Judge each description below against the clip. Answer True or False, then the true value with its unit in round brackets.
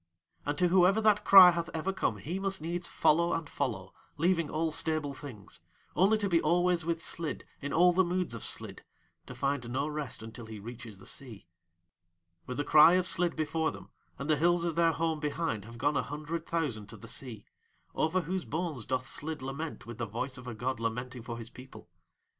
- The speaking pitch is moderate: True (150 Hz)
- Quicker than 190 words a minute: True (205 wpm)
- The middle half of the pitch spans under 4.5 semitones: False (5.5 semitones)